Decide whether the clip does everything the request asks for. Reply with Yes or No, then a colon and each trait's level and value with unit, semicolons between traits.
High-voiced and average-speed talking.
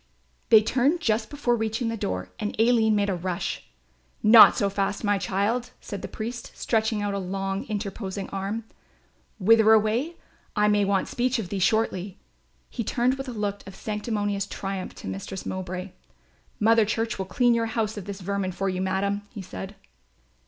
Yes: high, 205 Hz; average, 175 wpm